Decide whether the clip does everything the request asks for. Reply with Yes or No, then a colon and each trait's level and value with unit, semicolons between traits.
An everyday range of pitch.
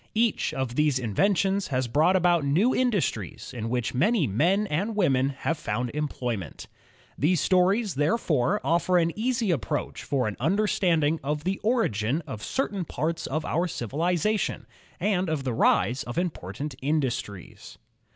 No: wide, 6.6 semitones